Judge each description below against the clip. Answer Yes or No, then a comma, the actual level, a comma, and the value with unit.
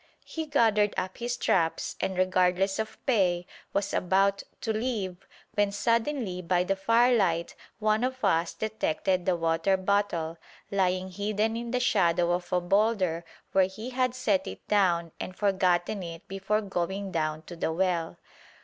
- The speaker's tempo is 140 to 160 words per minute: Yes, average, 155 wpm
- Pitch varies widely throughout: No, average, 3.4 semitones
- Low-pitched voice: No, high, 190 Hz